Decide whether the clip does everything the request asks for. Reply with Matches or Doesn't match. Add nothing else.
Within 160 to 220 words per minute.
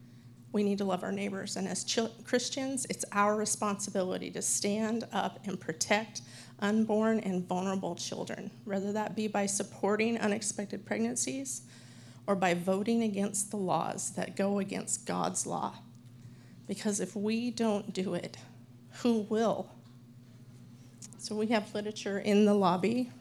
Doesn't match